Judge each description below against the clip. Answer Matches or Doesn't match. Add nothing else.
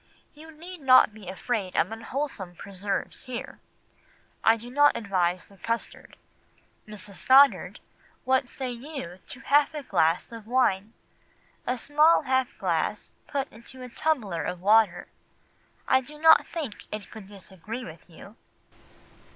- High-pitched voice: Matches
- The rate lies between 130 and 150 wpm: Matches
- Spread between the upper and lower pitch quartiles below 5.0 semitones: Doesn't match